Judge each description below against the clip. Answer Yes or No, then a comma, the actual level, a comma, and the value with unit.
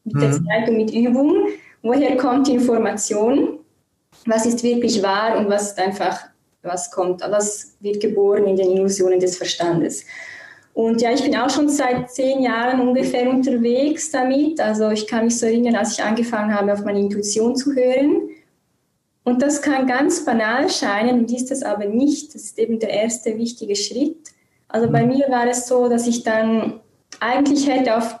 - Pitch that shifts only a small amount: No, average, 3.8 semitones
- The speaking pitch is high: Yes, high, 235 Hz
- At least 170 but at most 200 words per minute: Yes, average, 175 wpm